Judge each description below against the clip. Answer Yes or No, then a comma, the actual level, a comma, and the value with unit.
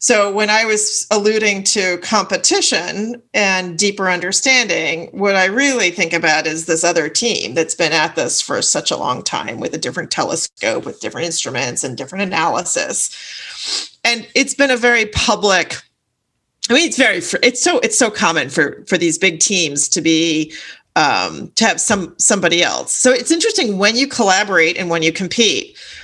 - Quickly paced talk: No, average, 175 wpm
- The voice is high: Yes, high, 200 Hz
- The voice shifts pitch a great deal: Yes, wide, 5.9 semitones